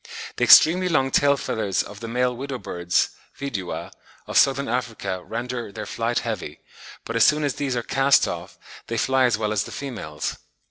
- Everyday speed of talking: Yes, average, 185 wpm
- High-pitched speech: No, low, 120 Hz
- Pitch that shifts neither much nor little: Yes, average, 4.2 semitones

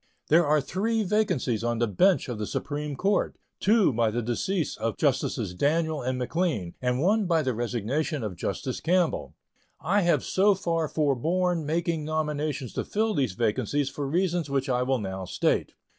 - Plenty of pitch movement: Yes, wide, 5.9 semitones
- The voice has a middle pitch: Yes, medium, 150 Hz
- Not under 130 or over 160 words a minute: No, average, 175 wpm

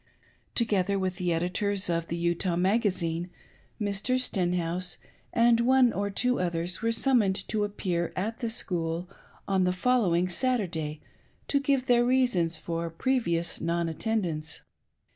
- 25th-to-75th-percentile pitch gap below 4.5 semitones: No, average, 5.1 semitones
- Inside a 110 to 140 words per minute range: Yes, slow, 135 wpm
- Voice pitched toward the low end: No, medium, 185 Hz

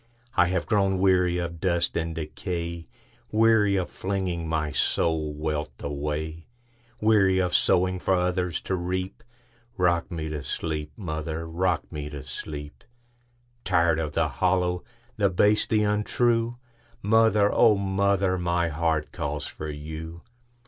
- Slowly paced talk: Yes, slow, 120 wpm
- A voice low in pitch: Yes, very low, 90 Hz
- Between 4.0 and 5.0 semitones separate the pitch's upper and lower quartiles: Yes, average, 4.4 semitones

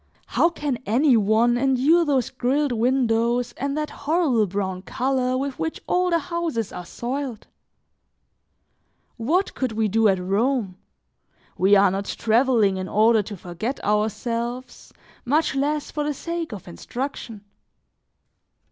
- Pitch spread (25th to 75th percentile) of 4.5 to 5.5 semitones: Yes, average, 4.8 semitones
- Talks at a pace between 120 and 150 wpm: Yes, slow, 135 wpm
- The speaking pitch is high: Yes, high, 245 Hz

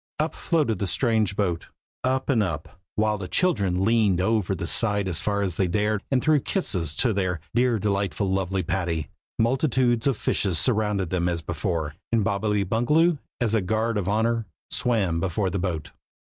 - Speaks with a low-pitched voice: Yes, low, 105 Hz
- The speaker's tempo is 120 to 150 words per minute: No, average, 175 wpm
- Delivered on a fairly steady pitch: No, average, 4.0 semitones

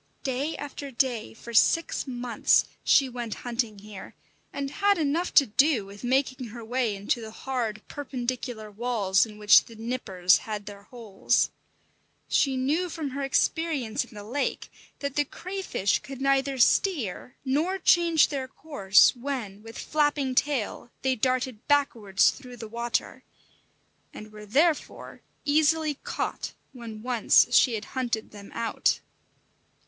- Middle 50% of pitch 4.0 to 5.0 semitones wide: Yes, average, 4.5 semitones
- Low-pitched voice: No, very high, 250 Hz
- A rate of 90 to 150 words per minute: Yes, average, 145 wpm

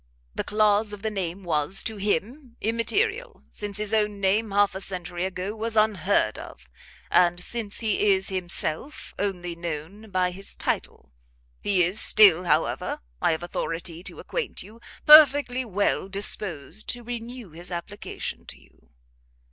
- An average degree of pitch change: Yes, average, 3.8 semitones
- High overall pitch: Yes, high, 200 Hz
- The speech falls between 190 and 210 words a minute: No, average, 150 wpm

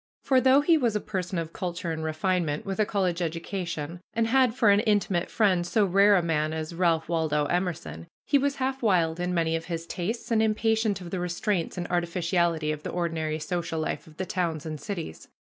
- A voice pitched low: No, medium, 175 Hz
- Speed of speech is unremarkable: No, fast, 210 wpm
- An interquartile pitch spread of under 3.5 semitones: No, average, 3.9 semitones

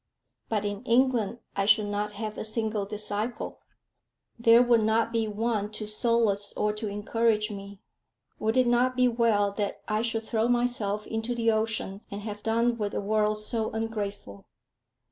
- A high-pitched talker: Yes, high, 220 Hz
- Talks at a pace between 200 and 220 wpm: No, average, 165 wpm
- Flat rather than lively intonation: Yes, narrow, 1.9 semitones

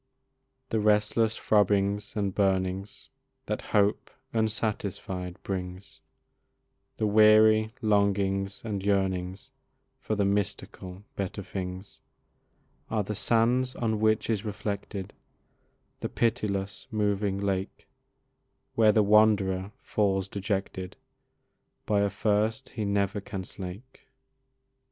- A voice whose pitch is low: Yes, low, 100 Hz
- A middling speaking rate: No, slow, 100 wpm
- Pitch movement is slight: Yes, narrow, 1.9 semitones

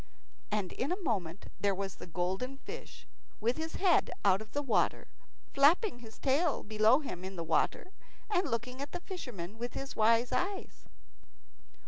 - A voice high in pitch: Yes, high, 240 Hz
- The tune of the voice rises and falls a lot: Yes, wide, 6.3 semitones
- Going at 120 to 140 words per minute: No, average, 165 wpm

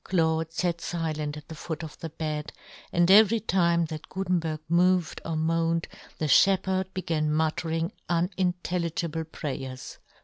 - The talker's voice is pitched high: No, medium, 165 Hz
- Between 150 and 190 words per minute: No, average, 140 wpm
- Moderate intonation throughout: No, narrow, 2.2 semitones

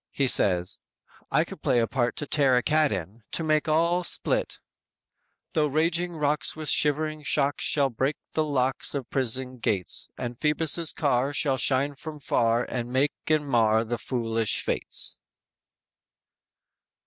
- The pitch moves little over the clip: No, average, 4.1 semitones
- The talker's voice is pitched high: No, medium, 140 Hz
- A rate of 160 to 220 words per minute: No, average, 150 wpm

